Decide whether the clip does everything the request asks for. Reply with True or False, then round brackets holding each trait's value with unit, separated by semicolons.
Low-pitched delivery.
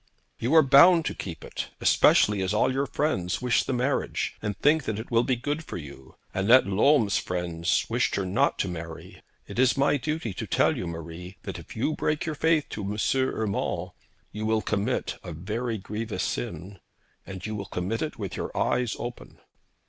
True (110 Hz)